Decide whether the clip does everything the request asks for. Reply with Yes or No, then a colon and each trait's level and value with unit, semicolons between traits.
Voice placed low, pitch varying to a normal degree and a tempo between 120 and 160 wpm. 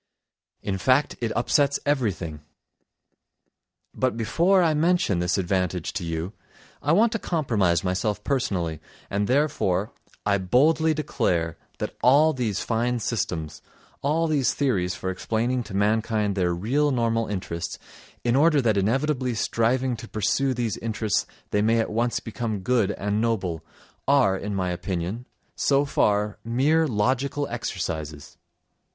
No: low, 115 Hz; wide, 5.8 semitones; slow, 135 wpm